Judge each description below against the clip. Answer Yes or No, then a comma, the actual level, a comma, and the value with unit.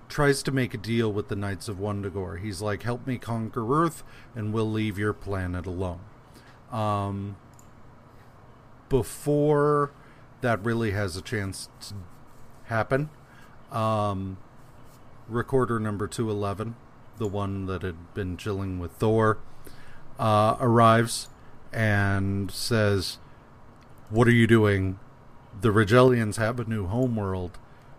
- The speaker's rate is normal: No, slow, 120 wpm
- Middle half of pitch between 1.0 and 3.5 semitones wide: Yes, average, 3.1 semitones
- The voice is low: Yes, low, 115 Hz